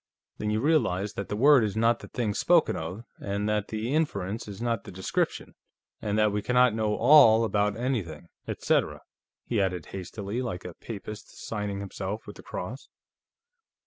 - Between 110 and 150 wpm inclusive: No, average, 175 wpm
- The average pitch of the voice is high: No, low, 105 Hz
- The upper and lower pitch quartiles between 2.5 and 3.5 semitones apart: Yes, average, 2.9 semitones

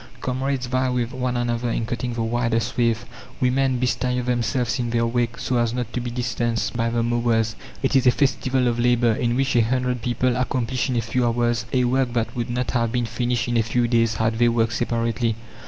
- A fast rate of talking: Yes, fast, 220 wpm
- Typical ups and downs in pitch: No, narrow, 1.3 semitones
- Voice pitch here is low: Yes, low, 120 Hz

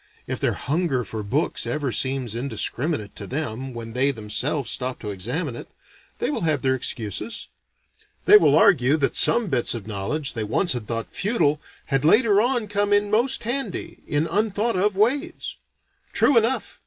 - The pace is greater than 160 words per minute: Yes, average, 170 wpm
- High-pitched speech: No, medium, 145 Hz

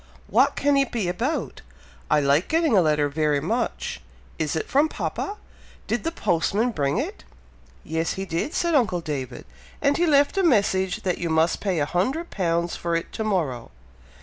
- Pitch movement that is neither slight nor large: No, wide, 9.0 semitones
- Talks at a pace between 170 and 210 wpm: Yes, average, 180 wpm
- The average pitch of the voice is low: No, medium, 185 Hz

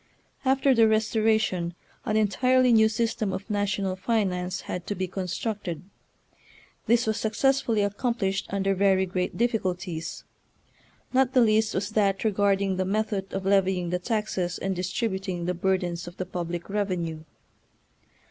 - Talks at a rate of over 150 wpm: No, average, 145 wpm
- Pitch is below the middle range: No, high, 195 Hz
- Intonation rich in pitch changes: No, average, 3.0 semitones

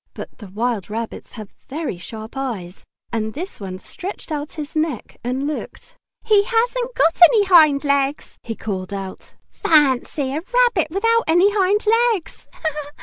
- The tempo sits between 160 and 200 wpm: No, average, 150 wpm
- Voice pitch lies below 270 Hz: No, very high, 300 Hz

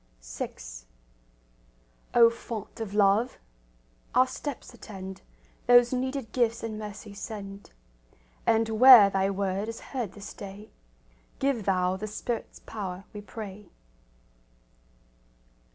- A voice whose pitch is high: Yes, high, 215 Hz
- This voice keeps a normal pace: No, slow, 110 wpm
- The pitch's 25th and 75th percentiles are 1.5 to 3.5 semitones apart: Yes, average, 3.0 semitones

